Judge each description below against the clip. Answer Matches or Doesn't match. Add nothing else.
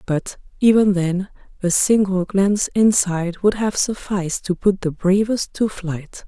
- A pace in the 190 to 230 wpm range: Doesn't match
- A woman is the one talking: Matches